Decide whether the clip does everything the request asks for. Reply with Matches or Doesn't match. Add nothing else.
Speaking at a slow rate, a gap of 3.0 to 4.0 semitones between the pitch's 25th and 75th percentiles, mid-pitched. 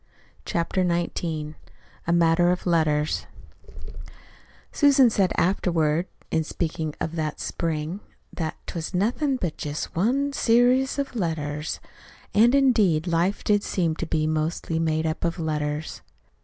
Doesn't match